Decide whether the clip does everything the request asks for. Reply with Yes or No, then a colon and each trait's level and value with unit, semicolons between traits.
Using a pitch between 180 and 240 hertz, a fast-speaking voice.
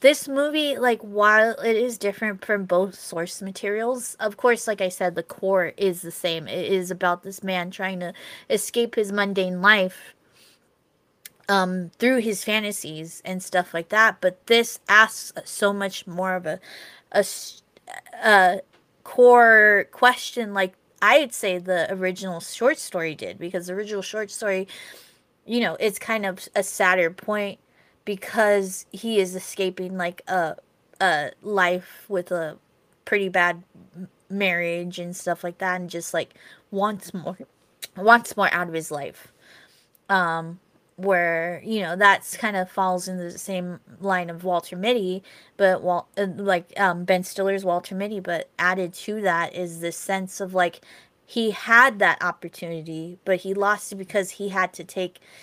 No: high, 190 Hz; average, 160 wpm